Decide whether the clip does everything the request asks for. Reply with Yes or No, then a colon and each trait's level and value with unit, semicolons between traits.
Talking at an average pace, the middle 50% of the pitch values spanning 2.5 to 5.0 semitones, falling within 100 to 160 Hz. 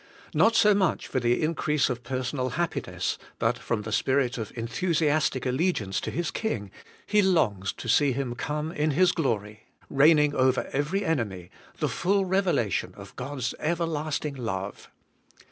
No: average, 150 wpm; wide, 5.6 semitones; medium, 140 Hz